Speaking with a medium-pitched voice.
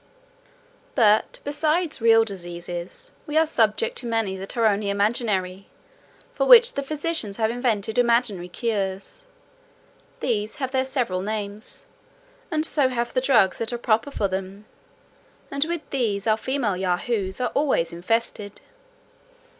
No: high, 225 Hz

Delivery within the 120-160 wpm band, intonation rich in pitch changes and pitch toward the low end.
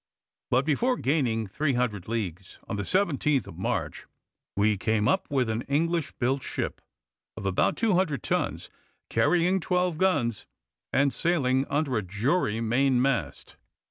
Yes: average, 140 wpm; wide, 6.3 semitones; low, 130 Hz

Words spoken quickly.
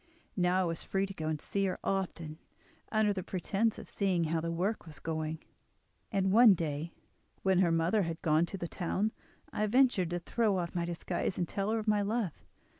Yes: fast, 210 wpm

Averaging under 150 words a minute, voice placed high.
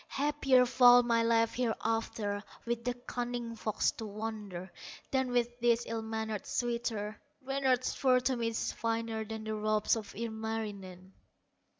Yes: average, 140 wpm; high, 230 Hz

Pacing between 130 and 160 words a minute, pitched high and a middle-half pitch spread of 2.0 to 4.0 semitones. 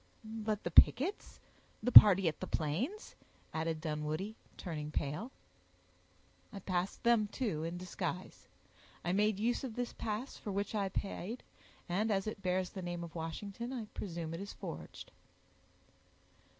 No: average, 145 wpm; high, 195 Hz; average, 4.4 semitones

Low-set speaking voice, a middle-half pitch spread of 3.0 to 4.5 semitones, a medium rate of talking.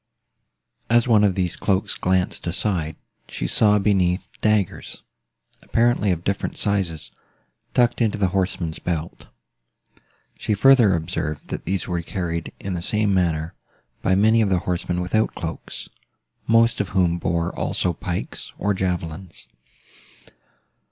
No: very low, 95 Hz; average, 3.3 semitones; slow, 130 wpm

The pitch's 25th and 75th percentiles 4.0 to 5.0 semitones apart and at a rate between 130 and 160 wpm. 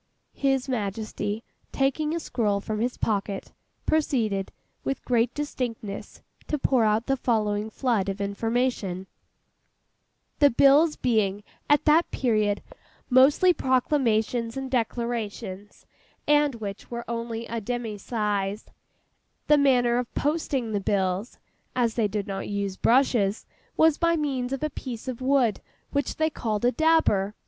Yes: average, 4.5 semitones; slow, 135 wpm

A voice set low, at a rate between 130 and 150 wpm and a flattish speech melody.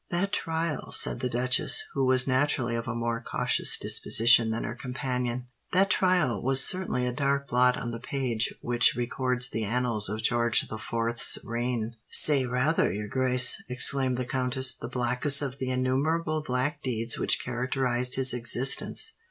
No: low, 125 Hz; average, 160 wpm; narrow, 2.2 semitones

